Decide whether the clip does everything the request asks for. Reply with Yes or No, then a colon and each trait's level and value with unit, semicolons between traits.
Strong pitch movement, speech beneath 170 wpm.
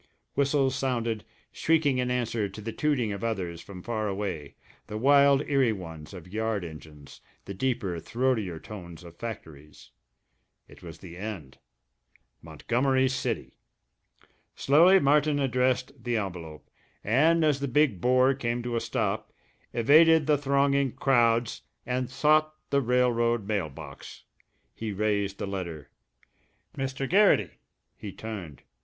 Yes: wide, 5.9 semitones; slow, 135 wpm